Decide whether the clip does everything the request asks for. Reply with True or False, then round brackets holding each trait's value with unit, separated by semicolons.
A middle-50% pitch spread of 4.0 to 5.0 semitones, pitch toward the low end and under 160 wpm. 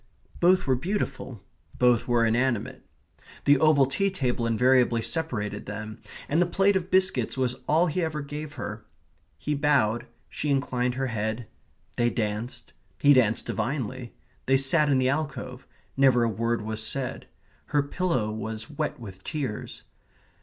True (4.4 semitones; 130 Hz; 150 wpm)